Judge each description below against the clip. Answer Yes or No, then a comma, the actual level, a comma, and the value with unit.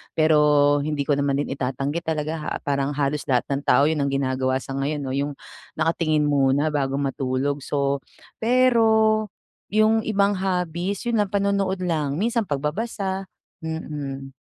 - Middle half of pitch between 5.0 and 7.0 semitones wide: Yes, wide, 5.4 semitones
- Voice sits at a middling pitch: Yes, medium, 150 Hz